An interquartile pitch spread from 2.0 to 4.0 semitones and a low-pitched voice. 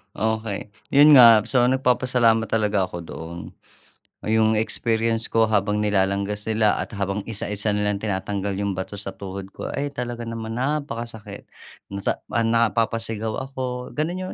Yes: narrow, 2.5 semitones; low, 110 Hz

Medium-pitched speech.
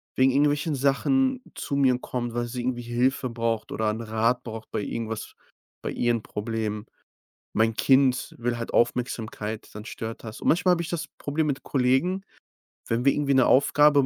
No: low, 125 Hz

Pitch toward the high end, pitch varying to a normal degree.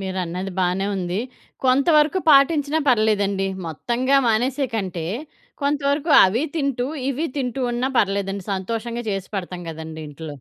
No: high, 220 Hz; wide, 6.5 semitones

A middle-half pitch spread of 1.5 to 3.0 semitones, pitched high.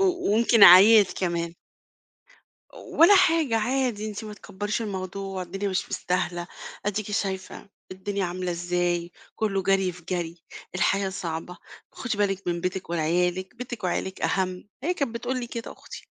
No: average, 3.4 semitones; high, 195 Hz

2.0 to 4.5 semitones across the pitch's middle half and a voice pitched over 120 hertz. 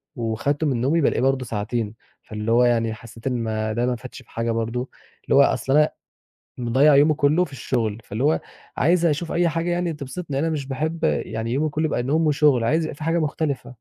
No: average, 5.0 semitones; low, 135 Hz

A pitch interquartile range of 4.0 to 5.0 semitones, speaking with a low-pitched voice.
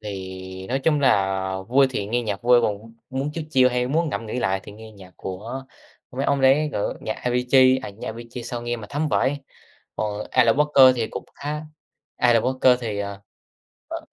Yes: average, 4.3 semitones; low, 120 Hz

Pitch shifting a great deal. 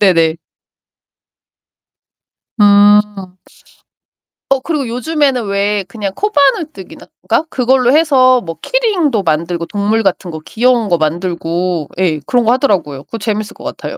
Yes: wide, 6.3 semitones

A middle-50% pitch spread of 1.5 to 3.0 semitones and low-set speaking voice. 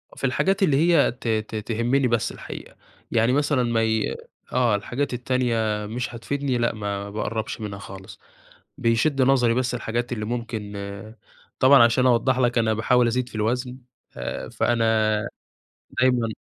Yes: narrow, 2.5 semitones; low, 120 Hz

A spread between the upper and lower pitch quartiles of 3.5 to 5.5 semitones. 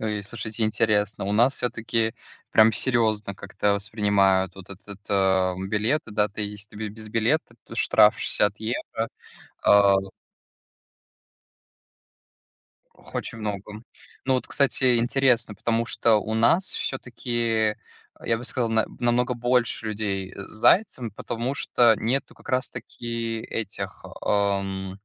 No: narrow, 2.5 semitones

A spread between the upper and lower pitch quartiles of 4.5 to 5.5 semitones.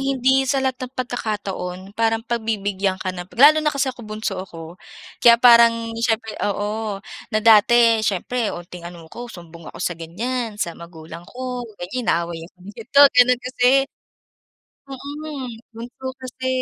Yes: average, 5.0 semitones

